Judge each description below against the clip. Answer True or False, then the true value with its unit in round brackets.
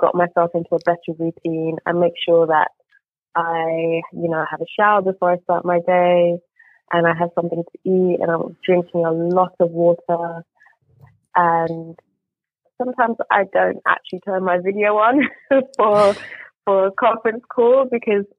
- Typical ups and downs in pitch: True (3.4 semitones)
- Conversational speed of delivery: True (160 wpm)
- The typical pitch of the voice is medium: True (175 Hz)